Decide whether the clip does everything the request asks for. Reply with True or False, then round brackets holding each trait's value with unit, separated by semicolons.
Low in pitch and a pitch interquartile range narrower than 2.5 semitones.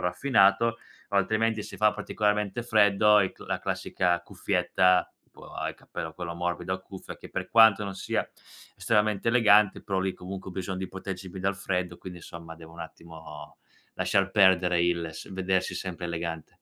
False (95 Hz; 2.9 semitones)